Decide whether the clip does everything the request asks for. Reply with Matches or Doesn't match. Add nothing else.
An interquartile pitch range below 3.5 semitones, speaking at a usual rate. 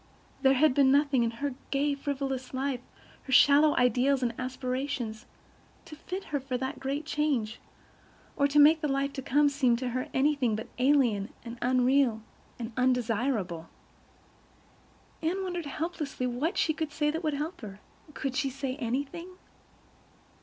Matches